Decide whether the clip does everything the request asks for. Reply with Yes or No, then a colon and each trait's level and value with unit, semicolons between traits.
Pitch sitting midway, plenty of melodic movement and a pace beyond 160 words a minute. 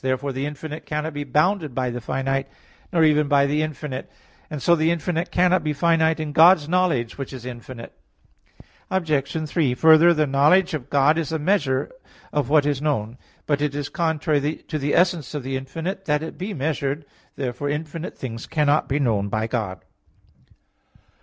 No: medium, 150 Hz; average, 3.0 semitones; average, 180 wpm